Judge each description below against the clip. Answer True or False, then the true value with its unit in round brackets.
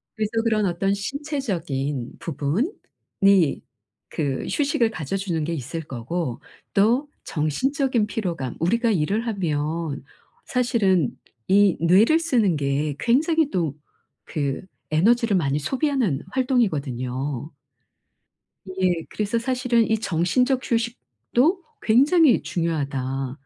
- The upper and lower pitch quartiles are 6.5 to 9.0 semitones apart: True (7.9 semitones)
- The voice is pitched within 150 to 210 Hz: True (190 Hz)